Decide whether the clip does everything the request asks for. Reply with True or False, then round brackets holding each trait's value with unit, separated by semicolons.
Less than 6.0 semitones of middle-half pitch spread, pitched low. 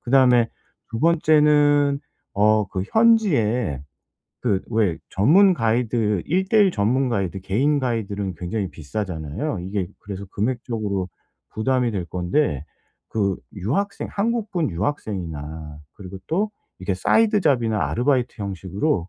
False (7.2 semitones; 110 Hz)